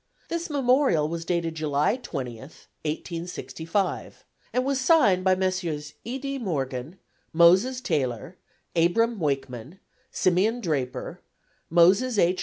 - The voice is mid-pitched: Yes, medium, 175 Hz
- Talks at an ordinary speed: No, slow, 110 wpm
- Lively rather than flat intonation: Yes, wide, 7.1 semitones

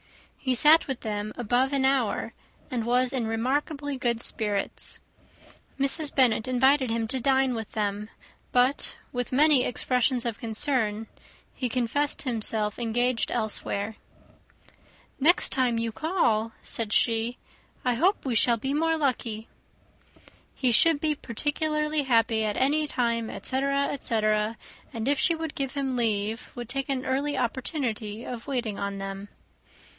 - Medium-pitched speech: No, high, 245 Hz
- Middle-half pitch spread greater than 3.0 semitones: Yes, average, 3.6 semitones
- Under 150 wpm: Yes, average, 140 wpm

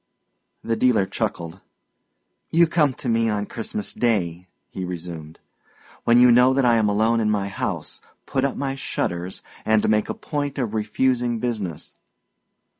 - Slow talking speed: No, average, 155 wpm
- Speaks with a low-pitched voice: Yes, low, 115 Hz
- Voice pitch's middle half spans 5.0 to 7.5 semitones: No, average, 4.1 semitones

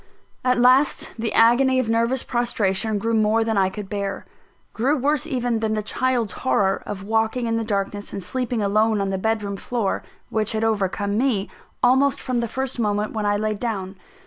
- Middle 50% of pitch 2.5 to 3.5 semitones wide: Yes, average, 3.0 semitones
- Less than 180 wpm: No, average, 195 wpm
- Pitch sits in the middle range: No, high, 220 Hz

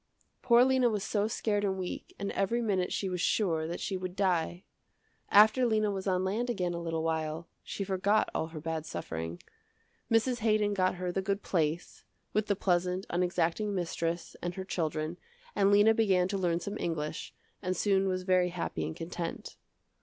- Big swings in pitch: No, average, 3.2 semitones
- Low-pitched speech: No, medium, 185 Hz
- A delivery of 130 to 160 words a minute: No, average, 185 wpm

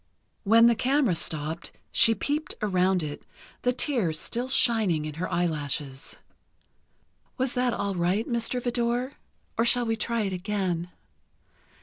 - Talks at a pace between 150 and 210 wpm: No, slow, 135 wpm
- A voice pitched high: Yes, high, 215 Hz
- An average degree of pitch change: No, wide, 5.7 semitones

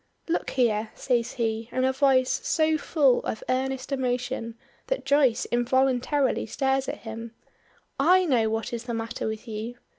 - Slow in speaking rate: No, average, 155 wpm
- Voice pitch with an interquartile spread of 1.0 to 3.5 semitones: Yes, average, 2.9 semitones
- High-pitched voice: Yes, very high, 250 Hz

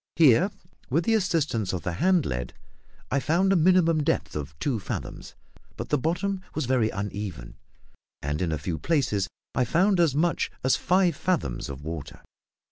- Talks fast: No, average, 170 wpm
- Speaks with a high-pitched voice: No, medium, 140 Hz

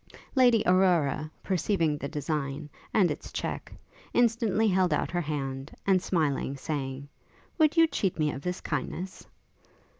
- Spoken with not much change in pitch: No, average, 5.0 semitones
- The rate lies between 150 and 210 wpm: No, average, 140 wpm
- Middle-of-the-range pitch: Yes, medium, 170 Hz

